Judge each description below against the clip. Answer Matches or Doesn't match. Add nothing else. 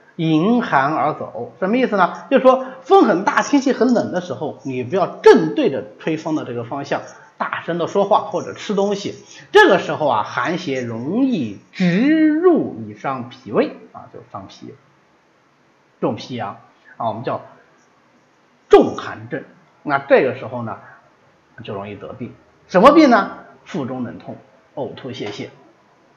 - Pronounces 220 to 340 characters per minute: Matches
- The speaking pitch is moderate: Doesn't match